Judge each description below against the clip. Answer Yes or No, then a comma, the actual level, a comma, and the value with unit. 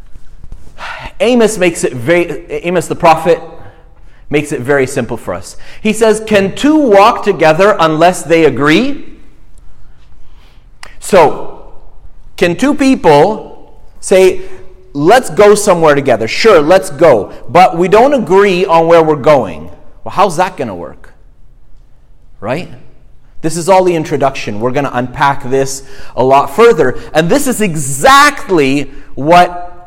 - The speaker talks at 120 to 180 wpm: Yes, slow, 135 wpm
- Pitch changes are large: Yes, wide, 6.5 semitones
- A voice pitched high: No, medium, 175 Hz